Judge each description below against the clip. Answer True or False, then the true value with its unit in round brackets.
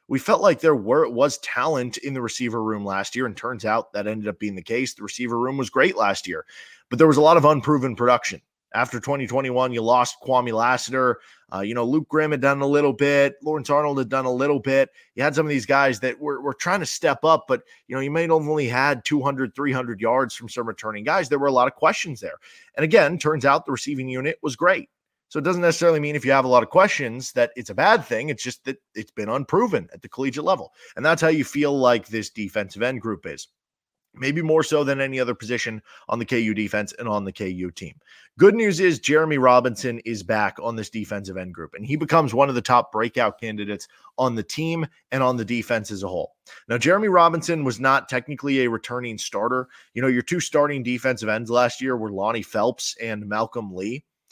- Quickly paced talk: True (235 wpm)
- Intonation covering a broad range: False (3.9 semitones)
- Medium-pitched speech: False (130 Hz)